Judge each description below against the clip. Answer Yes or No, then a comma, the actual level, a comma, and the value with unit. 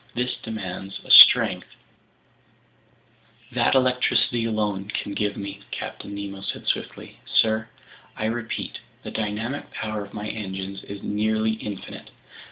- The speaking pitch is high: No, low, 105 Hz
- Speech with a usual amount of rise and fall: No, narrow, 1.8 semitones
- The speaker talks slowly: Yes, slow, 125 wpm